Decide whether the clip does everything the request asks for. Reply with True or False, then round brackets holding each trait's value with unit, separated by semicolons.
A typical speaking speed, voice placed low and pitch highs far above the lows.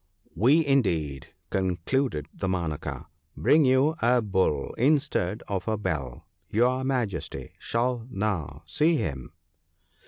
False (120 wpm; 105 Hz; 7.2 semitones)